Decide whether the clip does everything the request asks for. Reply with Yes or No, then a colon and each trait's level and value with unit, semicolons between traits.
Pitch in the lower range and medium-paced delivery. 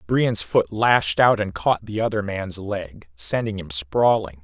Yes: low, 100 Hz; average, 175 wpm